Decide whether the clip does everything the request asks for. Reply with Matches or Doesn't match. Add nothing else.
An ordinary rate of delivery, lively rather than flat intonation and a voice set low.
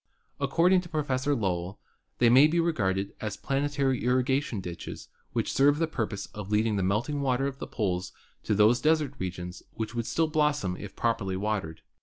Matches